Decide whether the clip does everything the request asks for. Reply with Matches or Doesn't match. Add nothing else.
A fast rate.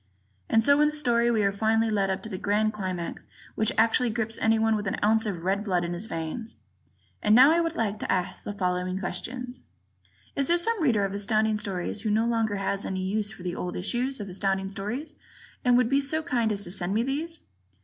Matches